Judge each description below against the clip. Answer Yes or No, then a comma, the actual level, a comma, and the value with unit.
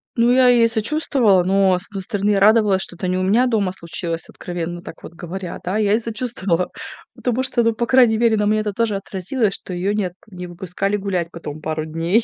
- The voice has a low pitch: No, high, 200 Hz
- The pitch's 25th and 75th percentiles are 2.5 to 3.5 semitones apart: No, average, 4.0 semitones